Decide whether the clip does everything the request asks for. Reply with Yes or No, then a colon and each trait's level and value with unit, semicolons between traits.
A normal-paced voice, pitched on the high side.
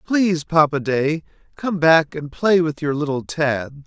No: average, 170 wpm; medium, 155 Hz